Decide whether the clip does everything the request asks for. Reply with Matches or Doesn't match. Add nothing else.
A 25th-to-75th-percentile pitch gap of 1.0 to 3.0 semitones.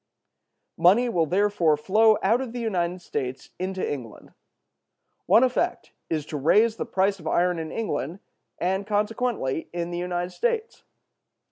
Doesn't match